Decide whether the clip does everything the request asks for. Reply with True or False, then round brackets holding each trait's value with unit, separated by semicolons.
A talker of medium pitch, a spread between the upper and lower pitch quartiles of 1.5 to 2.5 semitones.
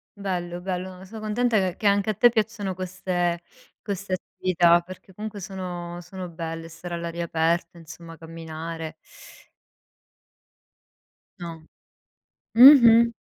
False (180 Hz; 2.9 semitones)